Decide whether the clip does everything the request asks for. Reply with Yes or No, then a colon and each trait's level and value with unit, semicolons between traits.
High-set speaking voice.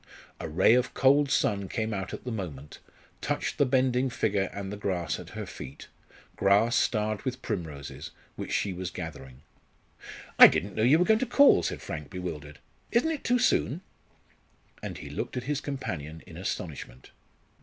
No: low, 105 Hz